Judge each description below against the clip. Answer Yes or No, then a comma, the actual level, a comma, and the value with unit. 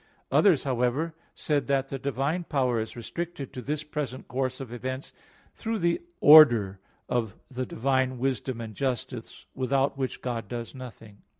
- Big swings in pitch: No, average, 2.7 semitones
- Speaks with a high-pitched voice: No, low, 130 Hz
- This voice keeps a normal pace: Yes, average, 155 wpm